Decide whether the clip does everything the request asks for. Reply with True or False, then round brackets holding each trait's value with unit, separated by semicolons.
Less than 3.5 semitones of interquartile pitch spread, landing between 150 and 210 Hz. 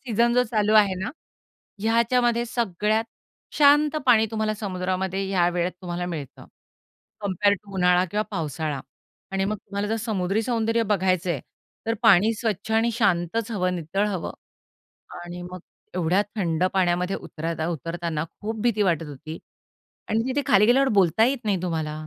False (4.2 semitones; 195 Hz)